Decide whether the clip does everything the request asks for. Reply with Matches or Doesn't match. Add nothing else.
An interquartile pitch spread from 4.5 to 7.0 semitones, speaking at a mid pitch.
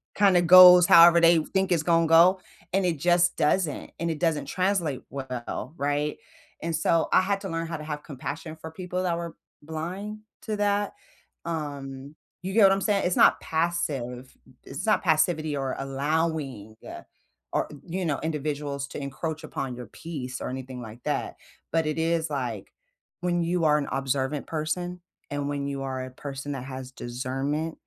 Doesn't match